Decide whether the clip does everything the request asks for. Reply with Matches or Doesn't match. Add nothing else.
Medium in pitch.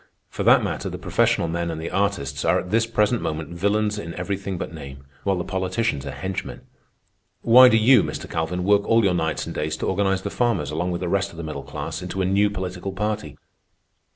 Doesn't match